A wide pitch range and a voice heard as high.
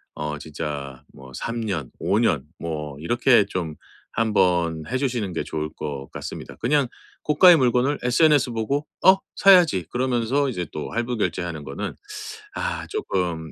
No: wide, 8.5 semitones; low, 105 Hz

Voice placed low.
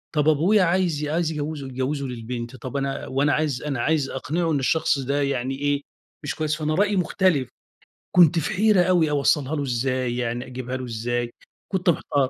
No: medium, 145 Hz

